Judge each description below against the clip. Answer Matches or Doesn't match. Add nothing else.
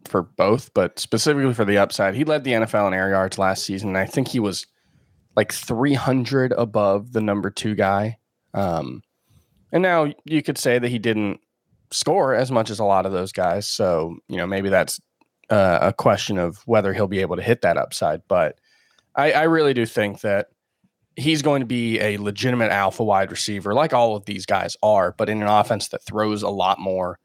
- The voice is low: Matches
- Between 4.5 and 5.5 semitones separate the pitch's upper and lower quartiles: Doesn't match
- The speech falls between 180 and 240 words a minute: Matches